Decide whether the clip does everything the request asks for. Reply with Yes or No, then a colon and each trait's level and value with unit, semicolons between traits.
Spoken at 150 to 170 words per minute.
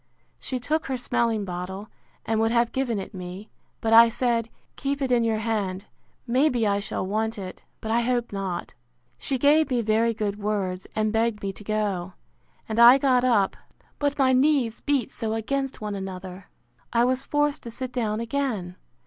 No: average, 185 wpm